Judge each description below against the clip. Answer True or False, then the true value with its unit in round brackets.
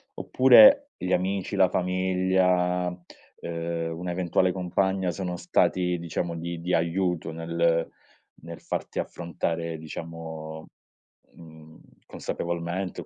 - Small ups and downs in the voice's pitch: True (1.8 semitones)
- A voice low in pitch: True (85 Hz)